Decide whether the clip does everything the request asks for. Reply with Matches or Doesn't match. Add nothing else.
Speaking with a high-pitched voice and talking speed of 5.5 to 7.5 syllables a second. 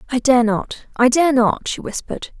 Doesn't match